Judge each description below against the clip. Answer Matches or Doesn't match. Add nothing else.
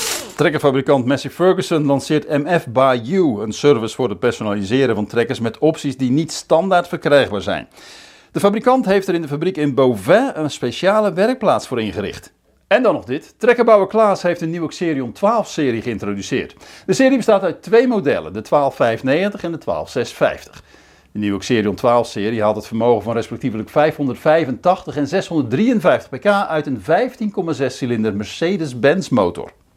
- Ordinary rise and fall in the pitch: Doesn't match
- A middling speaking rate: Matches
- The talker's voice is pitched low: Doesn't match